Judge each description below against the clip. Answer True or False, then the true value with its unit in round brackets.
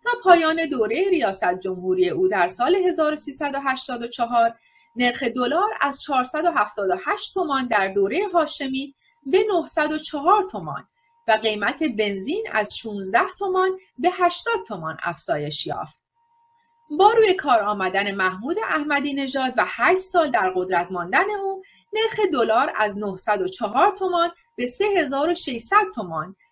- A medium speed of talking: True (120 wpm)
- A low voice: False (290 Hz)